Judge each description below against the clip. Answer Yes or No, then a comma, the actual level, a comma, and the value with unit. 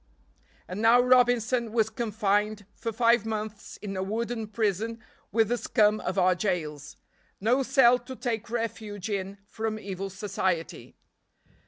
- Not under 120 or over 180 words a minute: Yes, average, 140 wpm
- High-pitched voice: Yes, high, 215 Hz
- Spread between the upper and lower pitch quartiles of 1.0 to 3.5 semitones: Yes, average, 2.8 semitones